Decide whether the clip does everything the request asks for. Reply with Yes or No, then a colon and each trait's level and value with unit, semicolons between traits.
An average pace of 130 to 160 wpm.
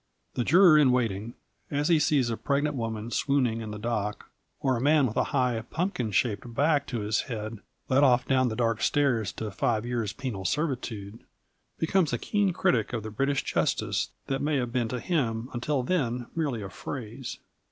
No: average, 190 wpm